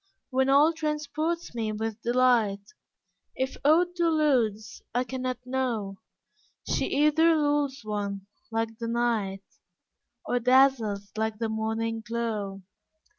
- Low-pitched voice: No, high, 235 Hz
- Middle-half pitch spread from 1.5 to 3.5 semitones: No, average, 4.3 semitones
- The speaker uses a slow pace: Yes, slow, 120 wpm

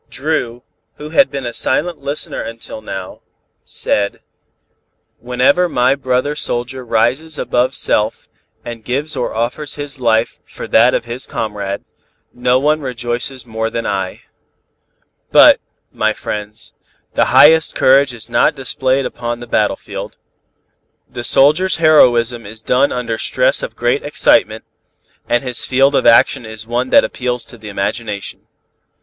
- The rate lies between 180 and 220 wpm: No, average, 140 wpm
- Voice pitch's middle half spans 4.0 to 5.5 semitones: No, average, 3.3 semitones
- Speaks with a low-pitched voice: Yes, low, 125 Hz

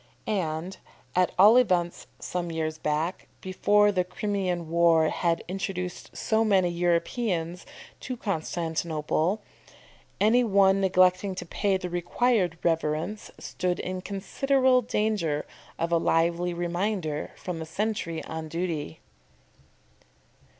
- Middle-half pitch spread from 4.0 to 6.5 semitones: No, average, 3.2 semitones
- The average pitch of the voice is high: No, medium, 180 Hz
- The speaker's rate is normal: No, slow, 115 wpm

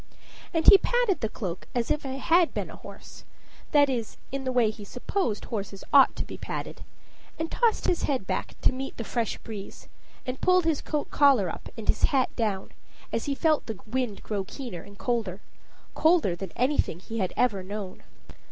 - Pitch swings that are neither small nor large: No, wide, 5.9 semitones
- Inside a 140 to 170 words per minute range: No, average, 195 wpm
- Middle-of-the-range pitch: No, high, 245 Hz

